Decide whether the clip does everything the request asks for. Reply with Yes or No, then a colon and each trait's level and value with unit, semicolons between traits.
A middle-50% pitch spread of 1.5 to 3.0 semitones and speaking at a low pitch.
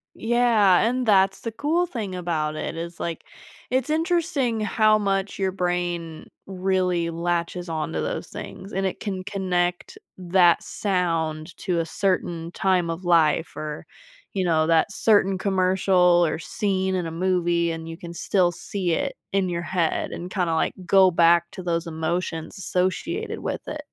No: narrow, 2.6 semitones; medium, 180 Hz